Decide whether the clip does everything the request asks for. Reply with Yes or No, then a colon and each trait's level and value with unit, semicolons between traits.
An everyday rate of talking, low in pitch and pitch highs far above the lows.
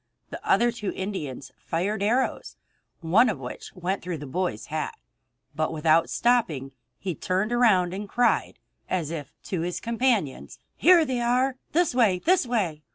No: average, 160 wpm; high, 195 Hz; wide, 6.5 semitones